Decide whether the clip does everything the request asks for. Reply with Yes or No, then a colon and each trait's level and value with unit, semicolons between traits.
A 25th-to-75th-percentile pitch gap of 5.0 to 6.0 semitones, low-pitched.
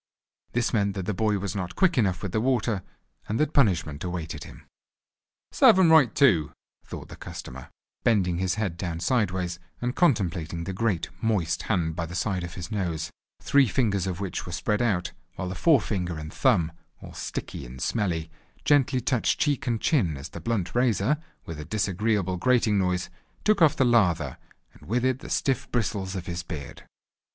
Yes: wide, 5.5 semitones; low, 100 Hz